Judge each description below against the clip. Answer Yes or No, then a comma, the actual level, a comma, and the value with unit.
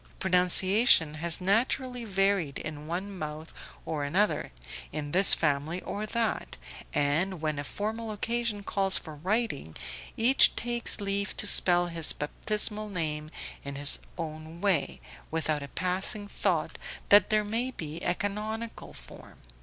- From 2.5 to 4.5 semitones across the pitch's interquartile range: No, average, 5.2 semitones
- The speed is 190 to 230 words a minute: No, average, 140 wpm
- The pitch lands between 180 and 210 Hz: Yes, medium, 185 Hz